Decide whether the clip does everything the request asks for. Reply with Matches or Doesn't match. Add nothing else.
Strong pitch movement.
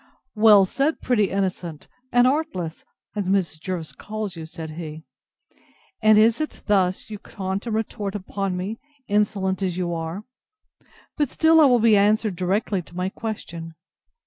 Doesn't match